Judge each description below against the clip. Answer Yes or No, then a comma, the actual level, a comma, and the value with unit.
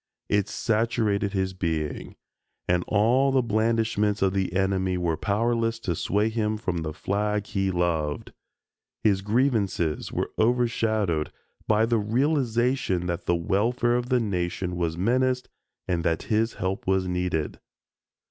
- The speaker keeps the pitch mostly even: No, average, 4.1 semitones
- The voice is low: Yes, low, 100 Hz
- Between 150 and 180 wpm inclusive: No, average, 140 wpm